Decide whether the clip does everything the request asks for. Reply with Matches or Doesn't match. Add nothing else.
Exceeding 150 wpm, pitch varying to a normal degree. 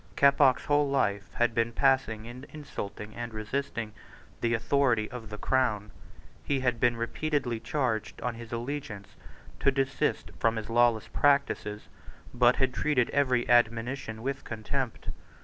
Doesn't match